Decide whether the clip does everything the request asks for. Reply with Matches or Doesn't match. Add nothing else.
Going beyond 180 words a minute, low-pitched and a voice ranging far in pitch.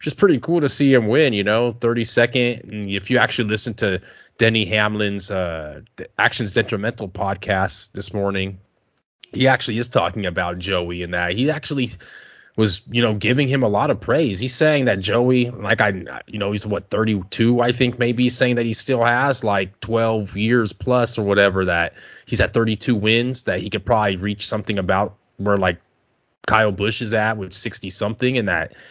Doesn't match